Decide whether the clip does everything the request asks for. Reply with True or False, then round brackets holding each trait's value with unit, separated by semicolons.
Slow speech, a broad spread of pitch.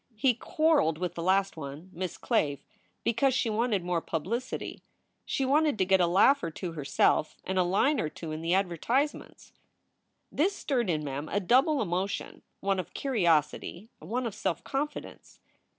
False (170 wpm; 7.1 semitones)